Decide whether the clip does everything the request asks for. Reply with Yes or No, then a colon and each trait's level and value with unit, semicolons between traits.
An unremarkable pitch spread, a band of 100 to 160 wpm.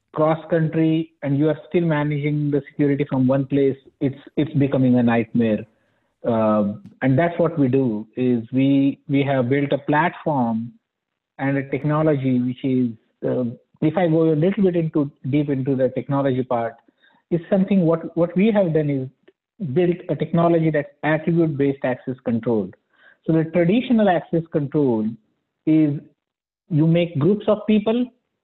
Yes: average, 3.9 semitones; average, 155 wpm